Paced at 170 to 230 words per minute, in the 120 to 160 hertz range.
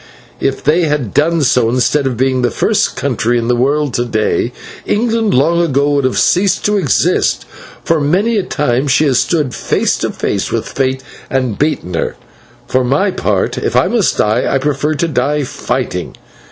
Yes: average, 185 wpm; medium, 140 Hz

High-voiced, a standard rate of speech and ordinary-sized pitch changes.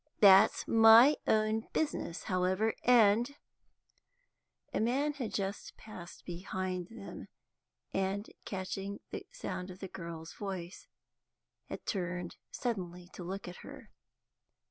No: high, 195 Hz; slow, 120 wpm; average, 3.5 semitones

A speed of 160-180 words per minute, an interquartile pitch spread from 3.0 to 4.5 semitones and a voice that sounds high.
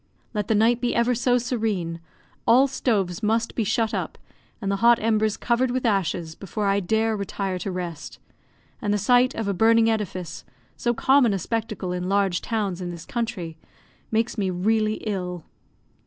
Yes: average, 175 wpm; average, 3.6 semitones; high, 215 Hz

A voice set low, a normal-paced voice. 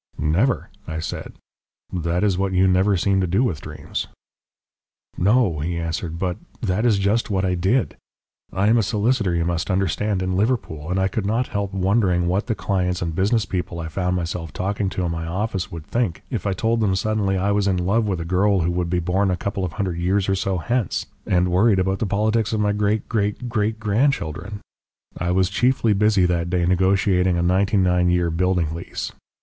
No: very low, 95 Hz; fast, 210 wpm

